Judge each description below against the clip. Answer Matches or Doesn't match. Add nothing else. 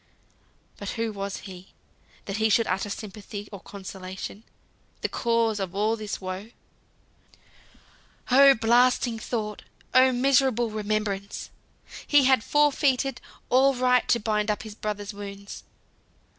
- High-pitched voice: Matches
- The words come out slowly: Matches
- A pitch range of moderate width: Matches